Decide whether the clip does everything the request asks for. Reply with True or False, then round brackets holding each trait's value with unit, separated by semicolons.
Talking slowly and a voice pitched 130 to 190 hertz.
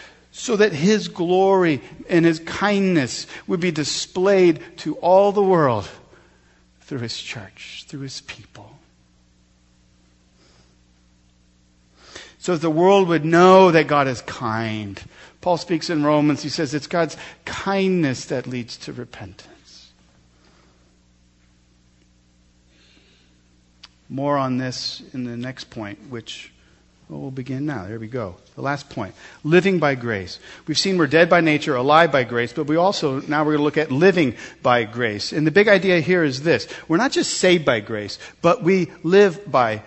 False (155 wpm; 135 Hz)